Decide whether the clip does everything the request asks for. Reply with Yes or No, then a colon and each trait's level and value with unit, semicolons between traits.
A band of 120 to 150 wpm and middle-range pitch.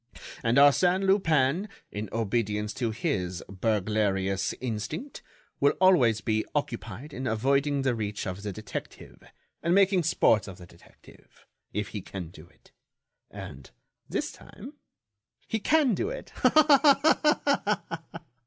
No: slow, 135 wpm; low, 120 Hz